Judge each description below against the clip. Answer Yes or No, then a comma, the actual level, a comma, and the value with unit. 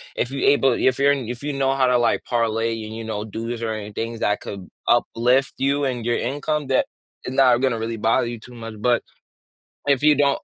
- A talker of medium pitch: No, low, 120 Hz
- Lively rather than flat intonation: No, average, 3.0 semitones